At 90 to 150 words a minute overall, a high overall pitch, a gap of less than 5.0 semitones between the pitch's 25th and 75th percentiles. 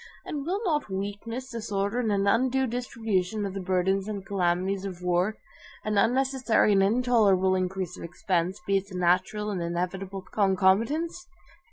Yes: average, 145 wpm; high, 200 Hz; average, 3.5 semitones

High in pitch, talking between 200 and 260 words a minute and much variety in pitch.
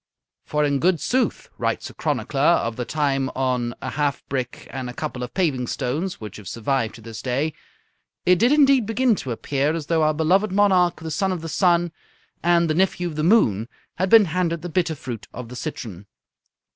No: medium, 155 Hz; fast, 205 wpm; wide, 6.2 semitones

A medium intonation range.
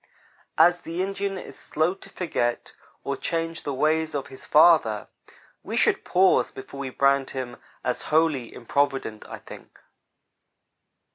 Yes: average, 4.0 semitones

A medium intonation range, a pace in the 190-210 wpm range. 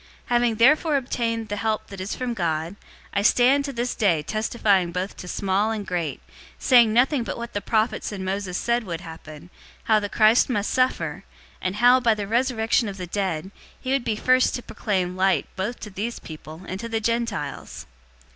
Yes: average, 4.0 semitones; average, 200 wpm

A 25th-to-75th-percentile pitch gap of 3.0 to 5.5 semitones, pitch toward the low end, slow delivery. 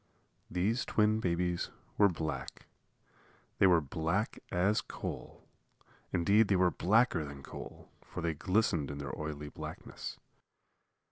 Yes: average, 4.5 semitones; very low, 90 Hz; slow, 125 wpm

